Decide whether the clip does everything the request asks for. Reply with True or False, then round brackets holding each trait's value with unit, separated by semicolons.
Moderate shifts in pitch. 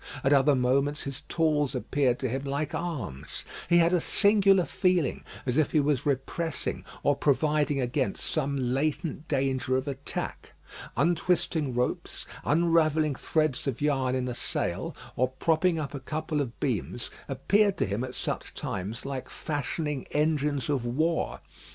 True (3.3 semitones)